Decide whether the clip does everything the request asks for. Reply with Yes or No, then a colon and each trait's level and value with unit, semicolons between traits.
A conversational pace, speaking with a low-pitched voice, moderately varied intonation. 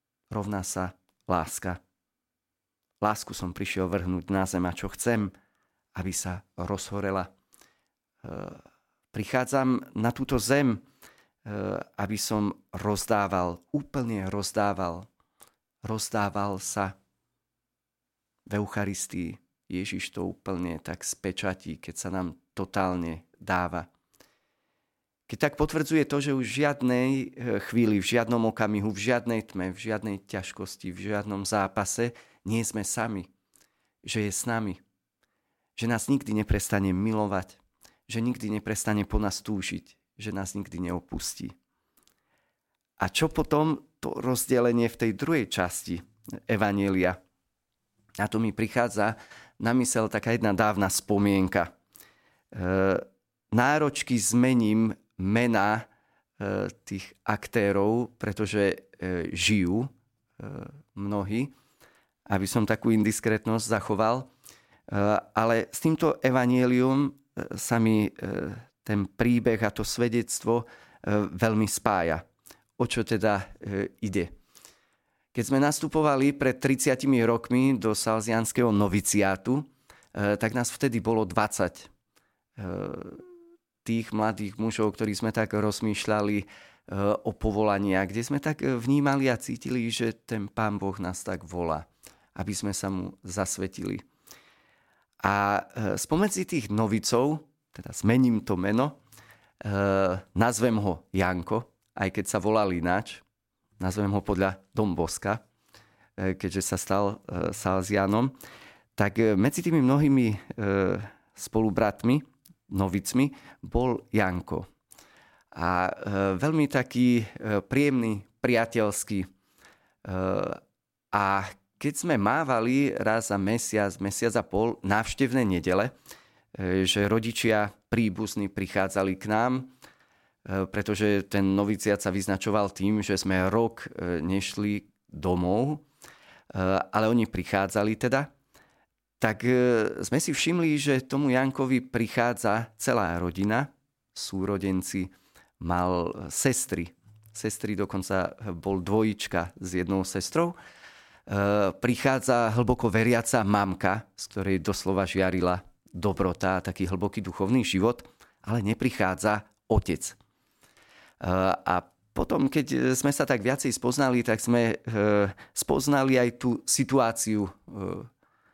No: slow, 105 wpm; low, 105 Hz; average, 3.7 semitones